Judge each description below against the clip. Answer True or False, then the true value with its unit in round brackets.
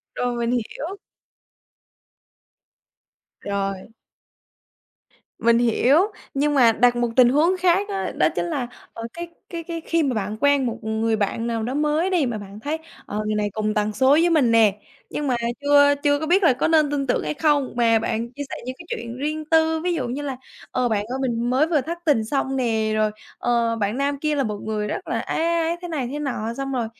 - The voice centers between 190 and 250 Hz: False (260 Hz)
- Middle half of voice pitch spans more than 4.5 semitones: True (4.9 semitones)